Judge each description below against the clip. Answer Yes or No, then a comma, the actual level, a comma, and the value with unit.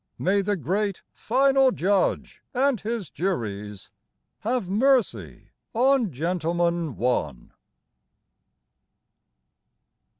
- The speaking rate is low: Yes, slow, 75 wpm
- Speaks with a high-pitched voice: Yes, high, 195 Hz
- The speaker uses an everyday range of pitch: No, wide, 6.5 semitones